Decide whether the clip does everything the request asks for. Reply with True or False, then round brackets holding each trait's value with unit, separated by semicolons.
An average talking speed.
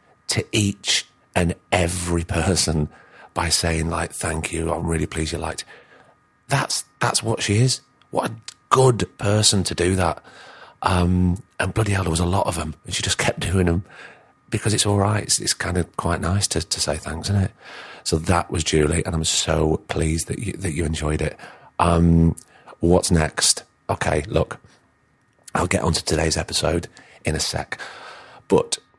True (180 wpm)